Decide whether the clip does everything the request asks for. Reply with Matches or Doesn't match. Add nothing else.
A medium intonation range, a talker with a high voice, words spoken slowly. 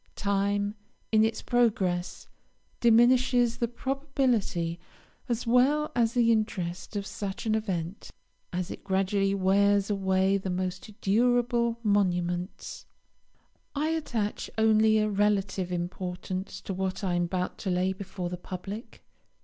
Matches